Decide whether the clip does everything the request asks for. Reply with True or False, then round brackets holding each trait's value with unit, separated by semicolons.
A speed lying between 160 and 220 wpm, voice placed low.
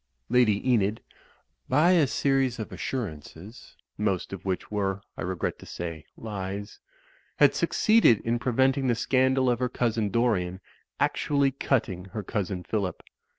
False (145 wpm; 110 Hz)